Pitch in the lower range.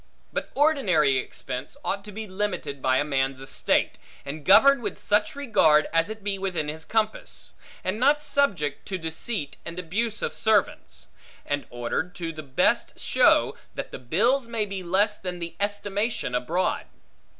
No: medium, 185 Hz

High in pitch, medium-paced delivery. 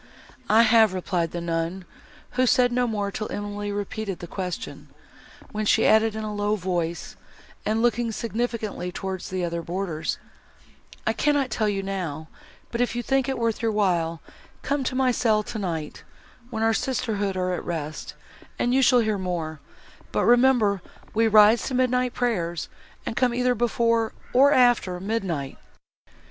Yes: high, 215 Hz; average, 160 wpm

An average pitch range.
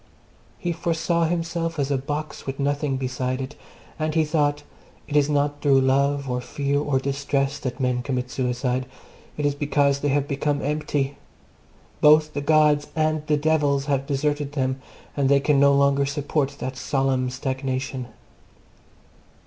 No: narrow, 1.8 semitones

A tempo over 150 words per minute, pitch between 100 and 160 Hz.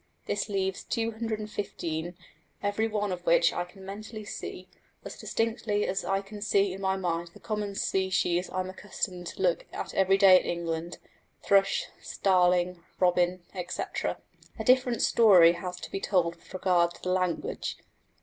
No: average, 160 wpm; high, 190 Hz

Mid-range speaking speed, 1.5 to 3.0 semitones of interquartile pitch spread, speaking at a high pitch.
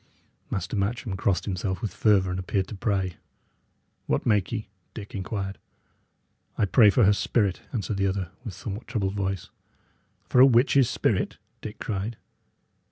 No: average, 160 wpm; narrow, 2.5 semitones; low, 100 Hz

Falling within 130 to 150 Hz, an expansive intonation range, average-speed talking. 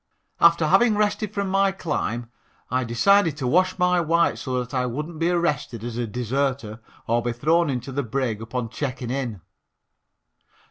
Yes: low, 135 Hz; wide, 6.1 semitones; average, 170 wpm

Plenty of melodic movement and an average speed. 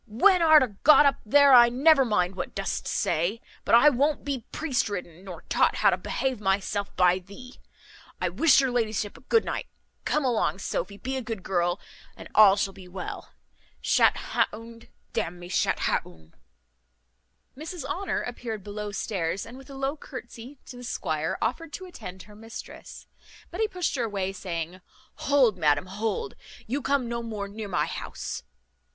Yes: wide, 5.8 semitones; average, 180 wpm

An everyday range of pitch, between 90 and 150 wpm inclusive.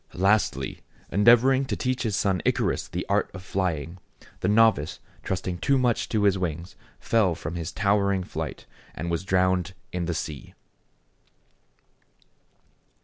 Yes: average, 3.9 semitones; average, 140 wpm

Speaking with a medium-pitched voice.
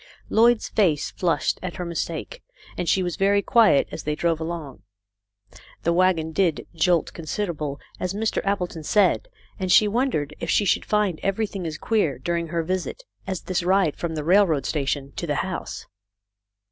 Yes: medium, 175 Hz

